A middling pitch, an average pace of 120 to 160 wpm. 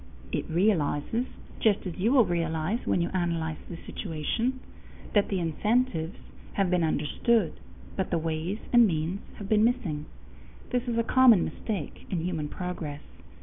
Yes: medium, 180 Hz; average, 150 wpm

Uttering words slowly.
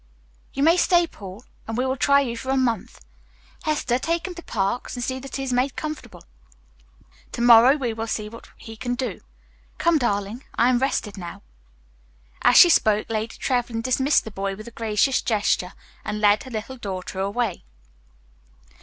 No: average, 180 wpm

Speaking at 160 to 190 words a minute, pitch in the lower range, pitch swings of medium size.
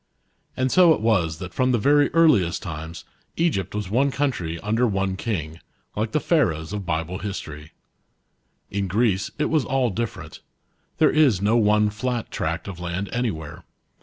No: average, 165 wpm; low, 105 Hz; wide, 6.1 semitones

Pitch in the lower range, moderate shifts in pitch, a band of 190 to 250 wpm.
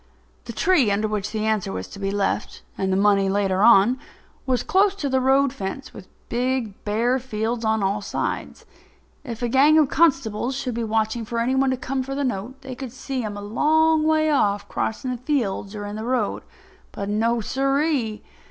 No: high, 235 Hz; average, 4.4 semitones; average, 195 wpm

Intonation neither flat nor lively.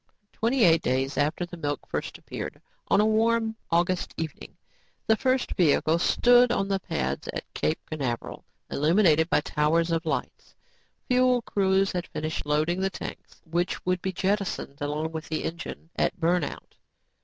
Yes: average, 4.2 semitones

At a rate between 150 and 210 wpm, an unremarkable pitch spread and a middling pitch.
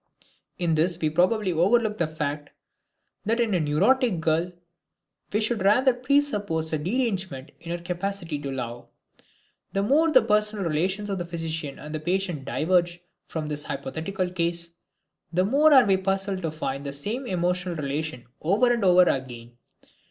Yes: average, 155 wpm; average, 4.8 semitones; medium, 180 Hz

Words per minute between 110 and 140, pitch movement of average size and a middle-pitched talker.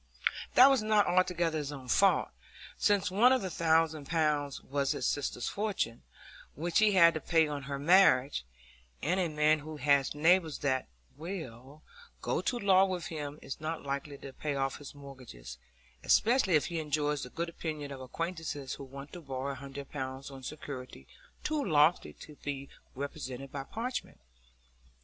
No: average, 170 wpm; average, 3.9 semitones; medium, 150 Hz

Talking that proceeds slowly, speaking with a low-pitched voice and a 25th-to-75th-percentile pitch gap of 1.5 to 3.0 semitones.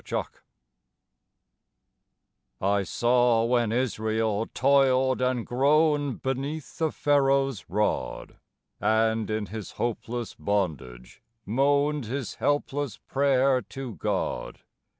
No: slow, 90 wpm; low, 125 Hz; average, 3.9 semitones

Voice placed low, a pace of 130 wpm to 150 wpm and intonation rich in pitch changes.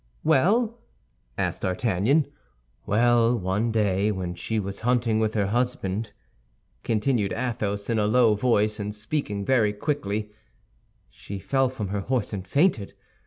No: low, 110 Hz; slow, 135 wpm; average, 3.4 semitones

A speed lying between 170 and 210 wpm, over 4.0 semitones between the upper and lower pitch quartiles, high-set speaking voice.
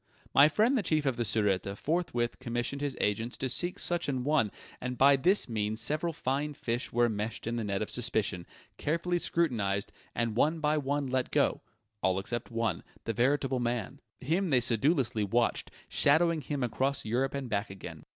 No: average, 180 wpm; average, 4.5 semitones; low, 125 Hz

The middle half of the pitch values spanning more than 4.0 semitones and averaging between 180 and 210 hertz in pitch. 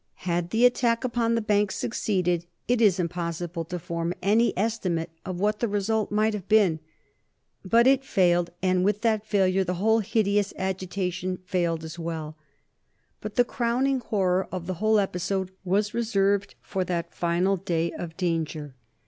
No: average, 3.7 semitones; high, 190 Hz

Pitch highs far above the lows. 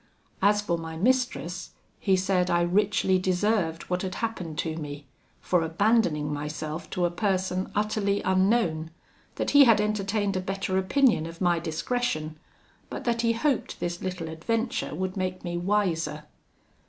No: average, 4.0 semitones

